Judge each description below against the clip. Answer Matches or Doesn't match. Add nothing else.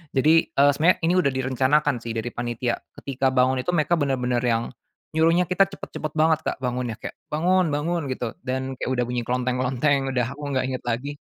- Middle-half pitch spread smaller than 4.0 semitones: Matches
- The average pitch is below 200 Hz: Matches